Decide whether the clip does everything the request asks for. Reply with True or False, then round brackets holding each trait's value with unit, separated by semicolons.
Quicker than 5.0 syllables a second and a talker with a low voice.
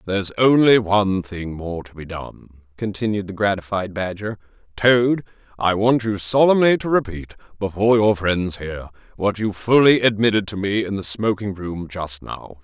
False (4.9 syllables/s; 100 Hz)